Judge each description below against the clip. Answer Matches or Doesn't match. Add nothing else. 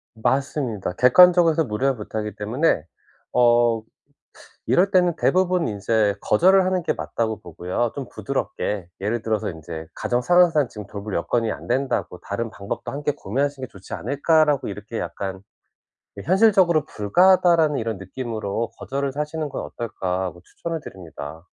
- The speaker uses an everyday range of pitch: Doesn't match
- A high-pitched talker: Doesn't match